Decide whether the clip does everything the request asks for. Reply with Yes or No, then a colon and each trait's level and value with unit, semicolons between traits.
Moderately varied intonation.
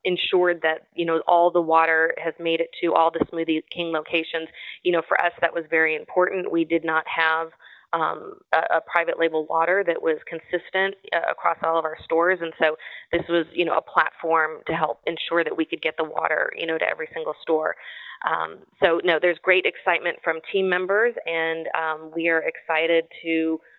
No: narrow, 1.6 semitones